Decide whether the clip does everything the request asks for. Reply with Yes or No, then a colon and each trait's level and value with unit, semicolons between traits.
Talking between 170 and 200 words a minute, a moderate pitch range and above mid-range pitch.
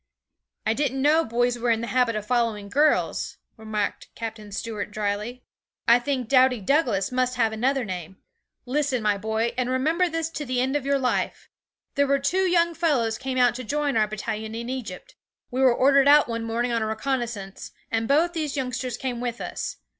Yes: average, 190 wpm; average, 3.8 semitones; high, 245 Hz